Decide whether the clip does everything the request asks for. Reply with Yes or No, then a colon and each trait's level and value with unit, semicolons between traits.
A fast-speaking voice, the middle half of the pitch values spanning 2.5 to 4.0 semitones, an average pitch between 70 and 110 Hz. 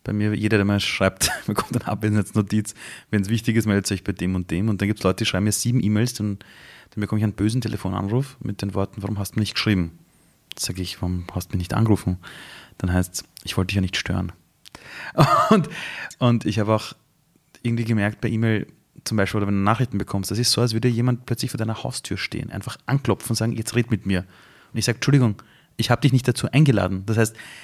Yes: fast, 240 wpm; average, 2.9 semitones; low, 105 Hz